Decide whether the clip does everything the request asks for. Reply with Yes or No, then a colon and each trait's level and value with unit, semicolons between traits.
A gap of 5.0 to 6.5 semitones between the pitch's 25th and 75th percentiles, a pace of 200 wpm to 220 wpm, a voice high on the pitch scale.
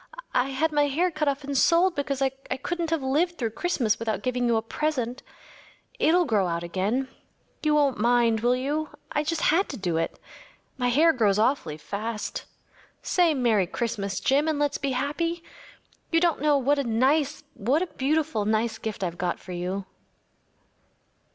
No: wide, 5.5 semitones; average, 170 wpm; very high, 265 Hz